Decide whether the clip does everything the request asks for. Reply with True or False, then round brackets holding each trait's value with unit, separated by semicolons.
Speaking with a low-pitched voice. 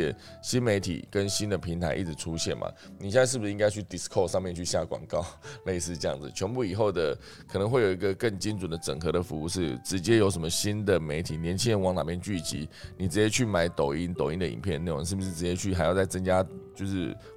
True (95 Hz)